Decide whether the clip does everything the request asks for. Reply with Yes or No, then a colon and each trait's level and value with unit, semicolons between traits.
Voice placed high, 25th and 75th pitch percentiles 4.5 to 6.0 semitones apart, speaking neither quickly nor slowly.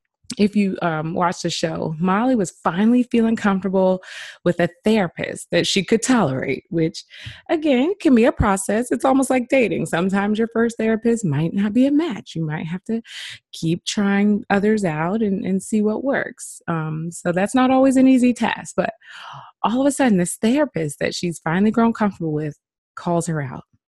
Yes: high, 200 Hz; average, 5.1 semitones; average, 185 wpm